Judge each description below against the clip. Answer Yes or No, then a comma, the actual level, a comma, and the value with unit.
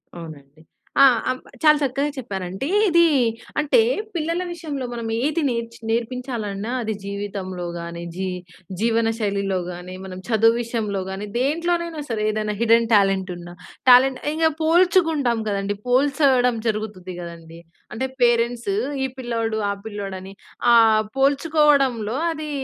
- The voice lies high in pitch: Yes, high, 230 Hz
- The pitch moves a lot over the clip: Yes, wide, 5.9 semitones